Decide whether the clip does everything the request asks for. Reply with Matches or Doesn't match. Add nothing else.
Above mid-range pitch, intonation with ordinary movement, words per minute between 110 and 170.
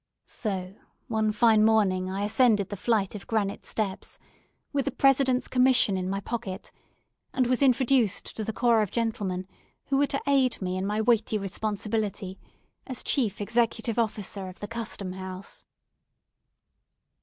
Matches